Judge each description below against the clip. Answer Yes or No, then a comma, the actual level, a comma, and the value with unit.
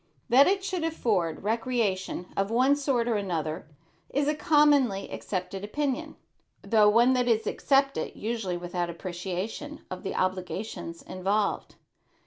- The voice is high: Yes, high, 215 Hz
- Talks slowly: Yes, slow, 130 wpm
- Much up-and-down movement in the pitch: Yes, wide, 6.4 semitones